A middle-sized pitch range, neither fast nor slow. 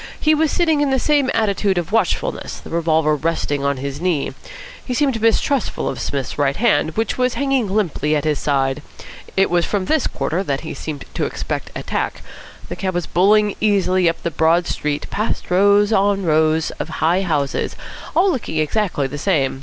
No: wide, 5.9 semitones; average, 185 wpm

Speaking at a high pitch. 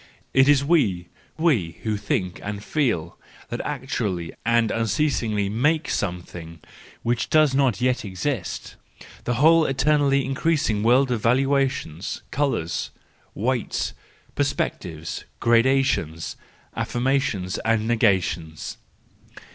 No: low, 115 Hz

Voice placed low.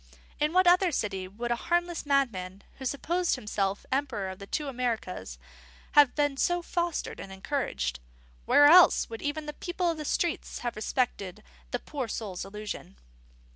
No: very high, 260 Hz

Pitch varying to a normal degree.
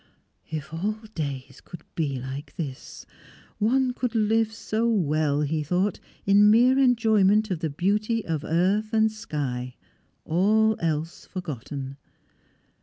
No: wide, 6.4 semitones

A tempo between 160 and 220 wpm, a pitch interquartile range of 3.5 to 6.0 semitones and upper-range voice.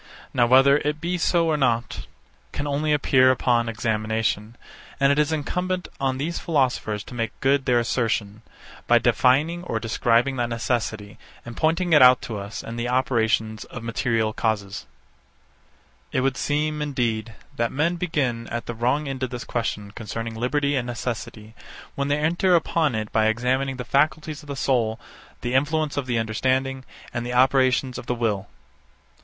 No: average, 170 wpm; average, 3.9 semitones; low, 125 Hz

